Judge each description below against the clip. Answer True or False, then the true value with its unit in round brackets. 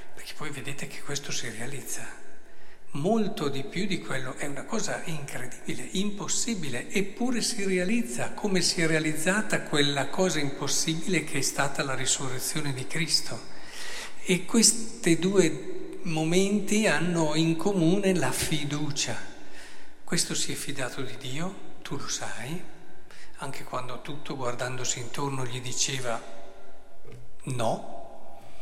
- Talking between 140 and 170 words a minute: False (125 wpm)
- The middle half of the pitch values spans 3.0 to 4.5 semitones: False (5.5 semitones)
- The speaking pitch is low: False (155 Hz)